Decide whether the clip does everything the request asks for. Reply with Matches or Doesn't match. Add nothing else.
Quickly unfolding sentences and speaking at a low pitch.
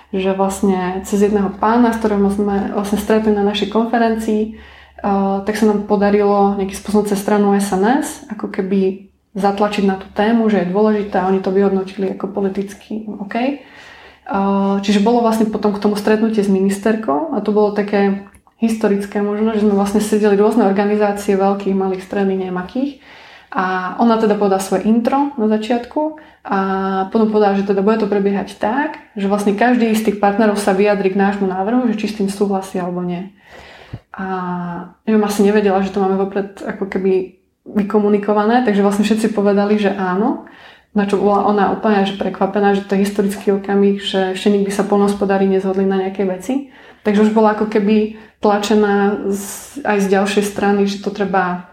Doesn't match